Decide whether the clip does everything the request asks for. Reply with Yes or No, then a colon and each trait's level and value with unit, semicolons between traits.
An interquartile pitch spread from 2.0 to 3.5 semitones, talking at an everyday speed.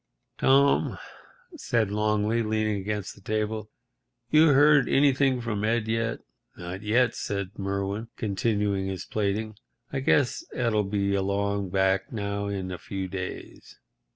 No: average, 2.7 semitones; slow, 130 wpm